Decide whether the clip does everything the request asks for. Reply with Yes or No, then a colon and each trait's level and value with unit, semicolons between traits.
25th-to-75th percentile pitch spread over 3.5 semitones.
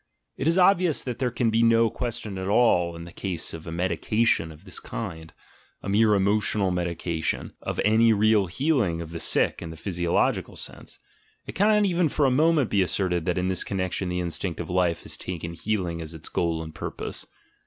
Yes: average, 5.2 semitones